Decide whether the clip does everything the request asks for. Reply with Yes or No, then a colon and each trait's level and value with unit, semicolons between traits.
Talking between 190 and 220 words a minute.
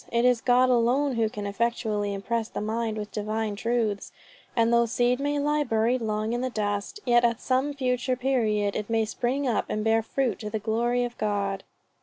Yes: average, 200 wpm